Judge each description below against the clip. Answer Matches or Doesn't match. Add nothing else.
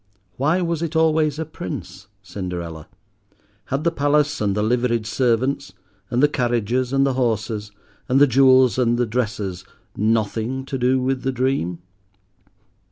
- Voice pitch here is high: Doesn't match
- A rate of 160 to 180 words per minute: Doesn't match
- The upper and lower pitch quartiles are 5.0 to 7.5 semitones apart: Doesn't match